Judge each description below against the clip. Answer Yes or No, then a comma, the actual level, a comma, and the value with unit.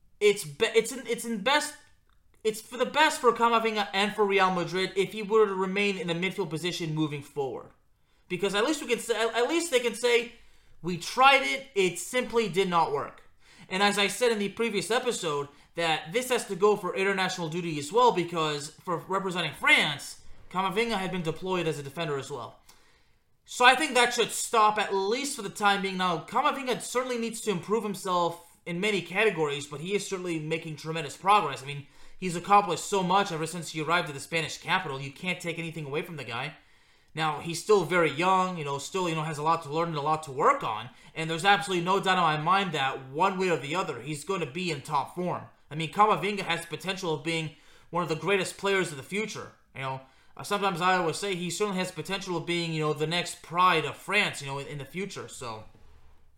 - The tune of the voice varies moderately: Yes, average, 4.5 semitones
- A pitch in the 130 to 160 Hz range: No, medium, 185 Hz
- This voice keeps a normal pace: No, fast, 225 wpm